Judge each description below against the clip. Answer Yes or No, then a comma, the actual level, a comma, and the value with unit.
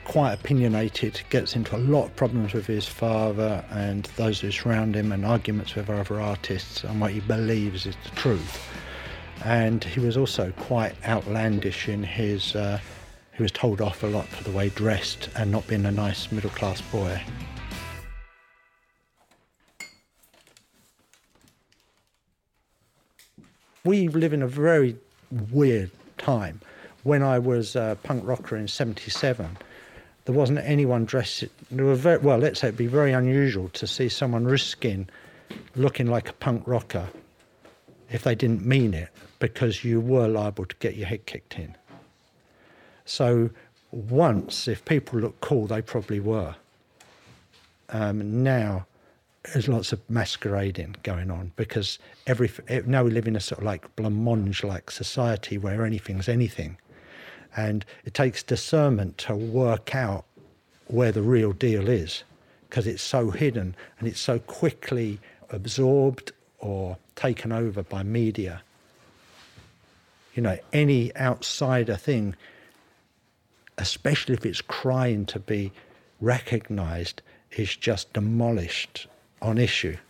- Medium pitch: No, low, 110 Hz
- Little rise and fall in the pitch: No, average, 3.6 semitones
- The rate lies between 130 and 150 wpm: Yes, average, 140 wpm